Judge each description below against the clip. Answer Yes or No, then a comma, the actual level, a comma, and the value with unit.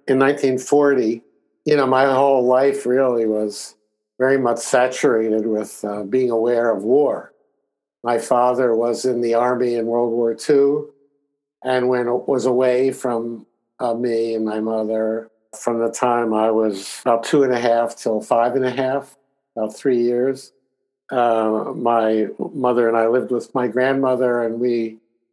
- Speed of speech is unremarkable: Yes, average, 160 wpm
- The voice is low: Yes, low, 120 Hz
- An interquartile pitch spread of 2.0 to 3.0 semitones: Yes, narrow, 2.5 semitones